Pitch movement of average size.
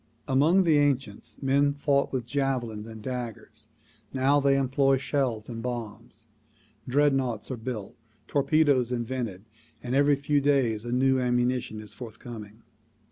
Yes: average, 3.1 semitones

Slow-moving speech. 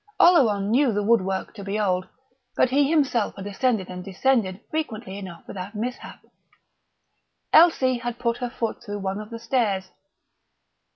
No: average, 155 wpm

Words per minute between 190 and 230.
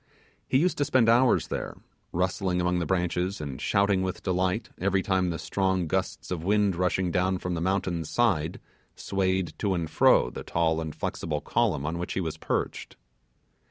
No: average, 180 wpm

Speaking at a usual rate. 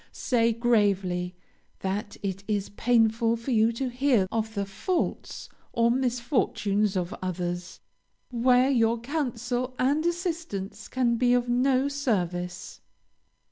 No: slow, 120 wpm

